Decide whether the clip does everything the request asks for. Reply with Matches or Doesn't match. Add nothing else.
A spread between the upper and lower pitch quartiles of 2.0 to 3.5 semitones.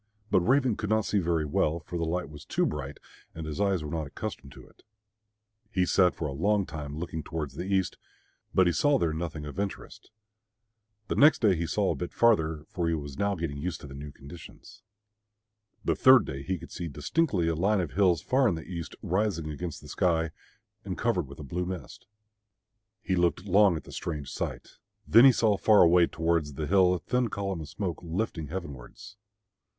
Doesn't match